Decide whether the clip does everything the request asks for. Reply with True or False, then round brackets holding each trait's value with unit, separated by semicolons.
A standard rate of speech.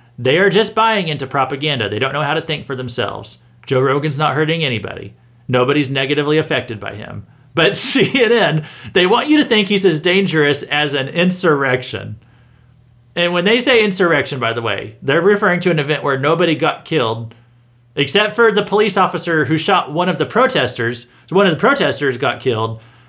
True (185 wpm)